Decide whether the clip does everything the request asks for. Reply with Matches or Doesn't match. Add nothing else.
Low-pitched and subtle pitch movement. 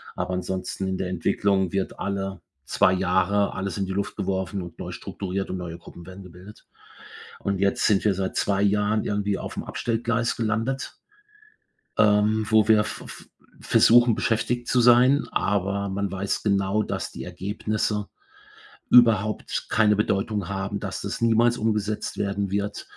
Matches